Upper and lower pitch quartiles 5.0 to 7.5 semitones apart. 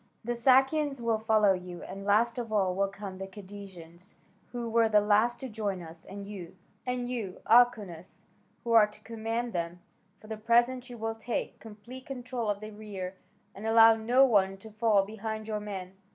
No: average, 3.1 semitones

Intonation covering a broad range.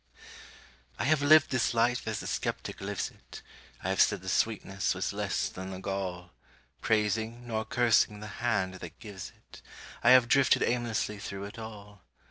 No: average, 3.5 semitones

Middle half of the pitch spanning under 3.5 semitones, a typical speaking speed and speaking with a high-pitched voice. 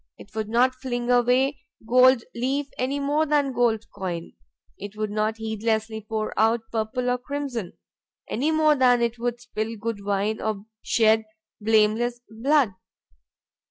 Yes: average, 2.8 semitones; average, 145 wpm; high, 235 Hz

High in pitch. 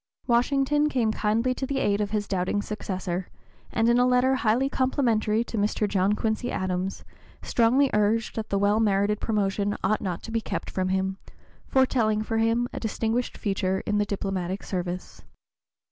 Yes: high, 215 Hz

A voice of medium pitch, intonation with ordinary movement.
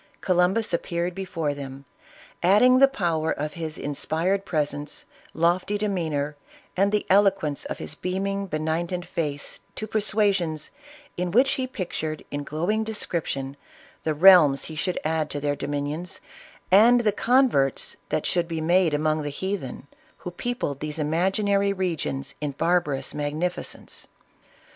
Yes: medium, 170 Hz; average, 4.7 semitones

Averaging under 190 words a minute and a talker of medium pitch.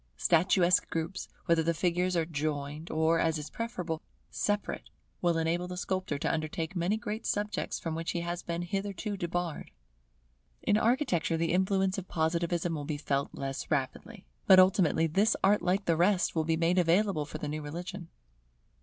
Yes: average, 170 wpm; medium, 170 Hz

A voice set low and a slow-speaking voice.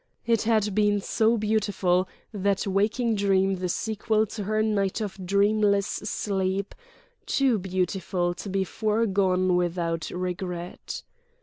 No: high, 200 Hz; slow, 120 wpm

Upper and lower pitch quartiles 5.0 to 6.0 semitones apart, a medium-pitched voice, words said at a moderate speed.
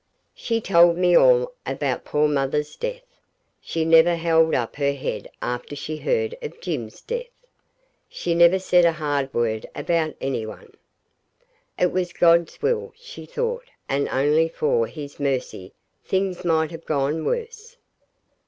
Yes: wide, 5.4 semitones; medium, 165 Hz; average, 145 wpm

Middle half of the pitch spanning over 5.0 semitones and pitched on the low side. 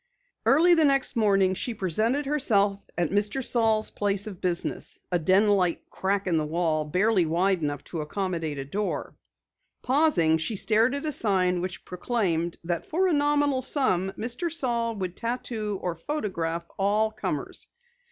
No: wide, 5.5 semitones; high, 200 Hz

